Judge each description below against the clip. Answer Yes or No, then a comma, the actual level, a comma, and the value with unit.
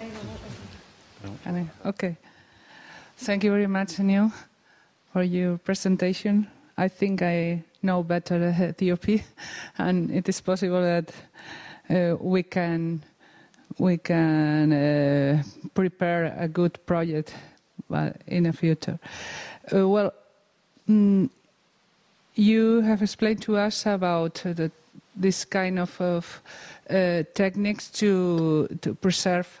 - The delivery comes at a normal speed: No, slow, 105 wpm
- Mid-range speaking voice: Yes, medium, 180 Hz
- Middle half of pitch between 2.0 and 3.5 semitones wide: Yes, average, 2.8 semitones